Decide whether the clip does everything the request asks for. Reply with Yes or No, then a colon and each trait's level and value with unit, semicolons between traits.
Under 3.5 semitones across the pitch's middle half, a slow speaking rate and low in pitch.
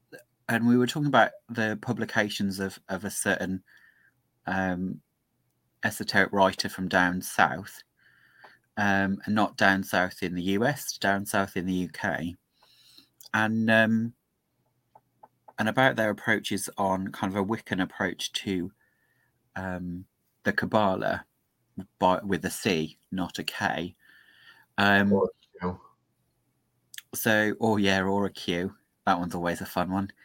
Yes: average, 2.9 semitones; slow, 130 wpm; low, 100 Hz